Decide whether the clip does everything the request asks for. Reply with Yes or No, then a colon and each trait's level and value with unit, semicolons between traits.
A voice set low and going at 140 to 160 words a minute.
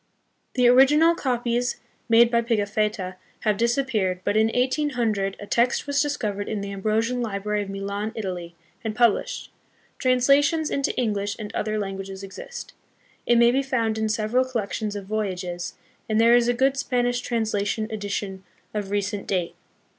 No: high, 220 Hz; average, 155 wpm